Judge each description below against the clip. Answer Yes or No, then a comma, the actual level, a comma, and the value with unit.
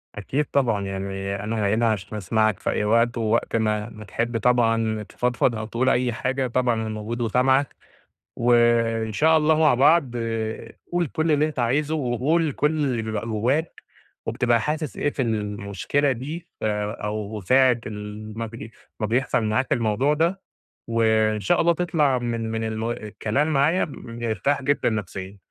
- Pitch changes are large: No, average, 3.8 semitones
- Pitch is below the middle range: Yes, low, 115 Hz